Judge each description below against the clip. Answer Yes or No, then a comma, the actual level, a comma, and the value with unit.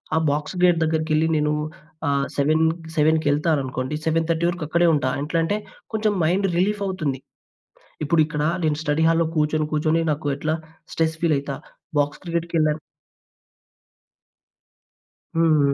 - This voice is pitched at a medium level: Yes, medium, 155 Hz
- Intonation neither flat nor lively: No, narrow, 2.0 semitones